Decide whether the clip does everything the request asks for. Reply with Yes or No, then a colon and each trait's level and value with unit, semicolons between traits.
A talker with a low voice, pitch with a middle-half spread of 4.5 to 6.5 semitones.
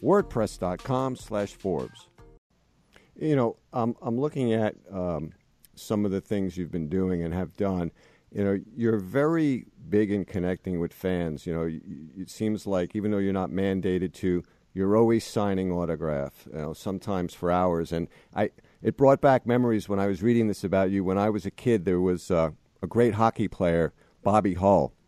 No: low, 100 Hz; average, 3.7 semitones